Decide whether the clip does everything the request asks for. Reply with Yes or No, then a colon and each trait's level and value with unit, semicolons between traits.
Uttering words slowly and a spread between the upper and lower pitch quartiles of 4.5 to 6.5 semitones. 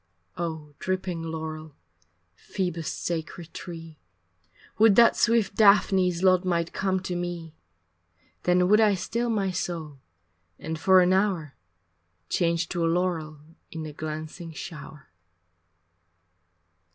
No: slow, 115 wpm; average, 2.8 semitones